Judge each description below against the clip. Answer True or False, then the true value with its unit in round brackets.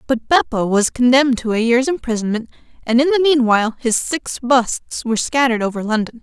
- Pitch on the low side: False (245 Hz)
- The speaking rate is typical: True (185 wpm)